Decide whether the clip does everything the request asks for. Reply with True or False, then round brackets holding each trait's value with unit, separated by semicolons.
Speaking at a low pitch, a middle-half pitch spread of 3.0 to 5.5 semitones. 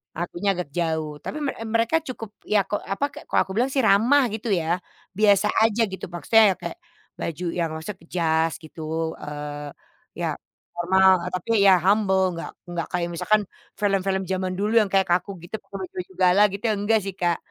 False (190 Hz; 3.6 semitones)